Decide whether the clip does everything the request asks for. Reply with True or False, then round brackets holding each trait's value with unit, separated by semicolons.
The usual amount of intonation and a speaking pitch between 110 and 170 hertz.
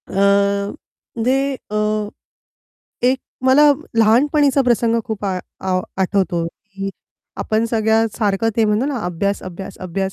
False (3.2 semitones; 210 Hz)